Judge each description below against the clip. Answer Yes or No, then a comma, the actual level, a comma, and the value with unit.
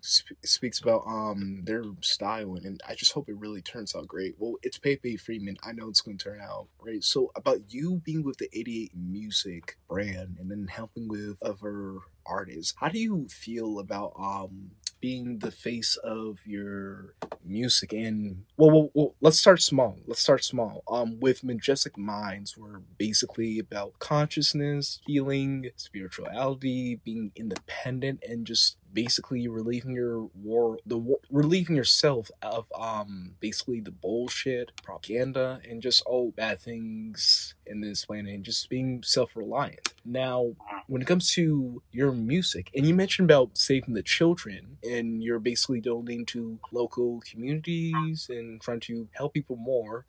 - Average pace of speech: Yes, average, 155 wpm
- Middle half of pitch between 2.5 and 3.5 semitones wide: No, average, 4.0 semitones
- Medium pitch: No, low, 115 Hz